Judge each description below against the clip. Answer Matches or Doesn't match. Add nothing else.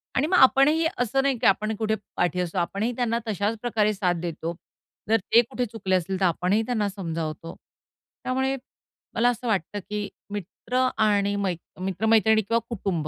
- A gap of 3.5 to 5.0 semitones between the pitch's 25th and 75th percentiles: Matches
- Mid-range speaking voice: Doesn't match